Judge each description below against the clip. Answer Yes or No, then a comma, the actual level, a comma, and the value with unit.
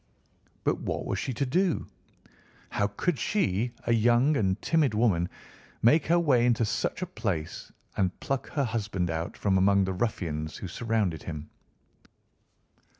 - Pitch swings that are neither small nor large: No, wide, 5.9 semitones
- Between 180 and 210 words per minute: No, average, 150 wpm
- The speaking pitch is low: Yes, low, 110 Hz